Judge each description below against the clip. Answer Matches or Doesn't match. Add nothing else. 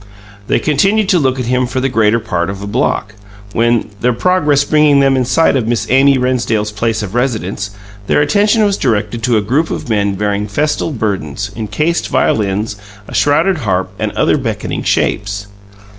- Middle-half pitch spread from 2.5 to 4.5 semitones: Doesn't match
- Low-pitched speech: Matches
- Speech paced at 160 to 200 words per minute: Matches